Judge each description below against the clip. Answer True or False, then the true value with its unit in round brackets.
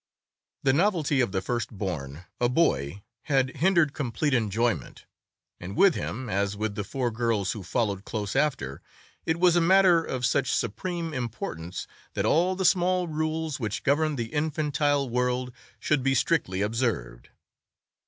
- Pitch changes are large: True (7.1 semitones)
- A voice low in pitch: True (125 Hz)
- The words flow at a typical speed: True (155 wpm)